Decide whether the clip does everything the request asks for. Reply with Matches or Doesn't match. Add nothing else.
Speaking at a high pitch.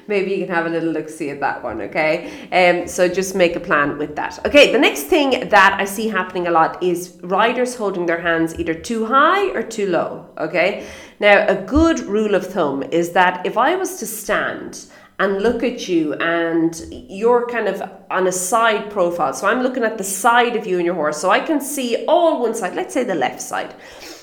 Matches